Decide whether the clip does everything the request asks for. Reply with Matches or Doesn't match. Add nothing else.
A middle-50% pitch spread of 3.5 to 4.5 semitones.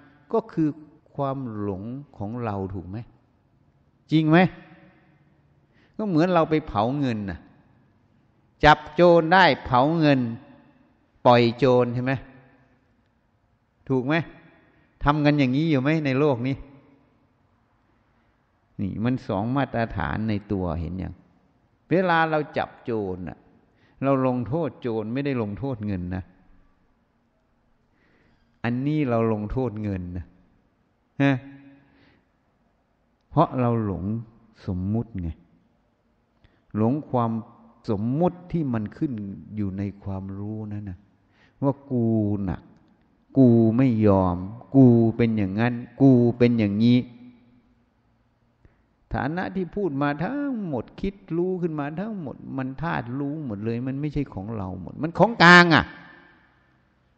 Doesn't match